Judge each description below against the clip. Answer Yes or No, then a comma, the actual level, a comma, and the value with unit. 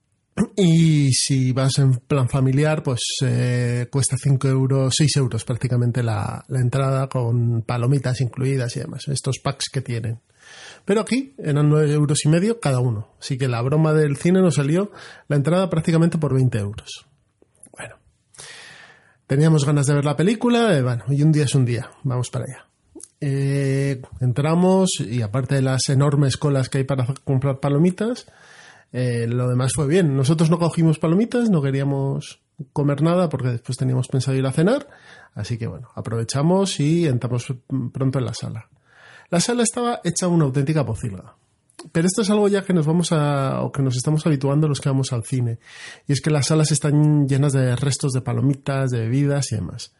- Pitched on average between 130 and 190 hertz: Yes, medium, 140 Hz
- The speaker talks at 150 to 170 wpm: No, average, 180 wpm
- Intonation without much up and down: No, average, 3.4 semitones